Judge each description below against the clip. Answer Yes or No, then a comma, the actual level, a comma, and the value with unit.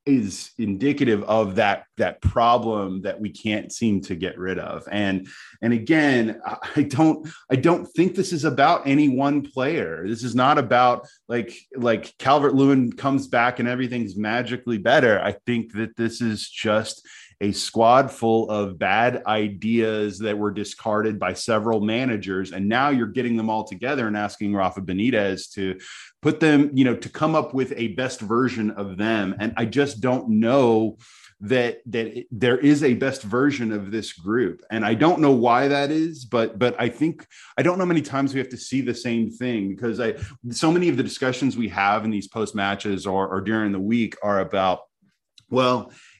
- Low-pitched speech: Yes, low, 115 Hz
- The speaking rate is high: No, average, 190 wpm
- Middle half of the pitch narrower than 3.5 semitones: No, average, 3.8 semitones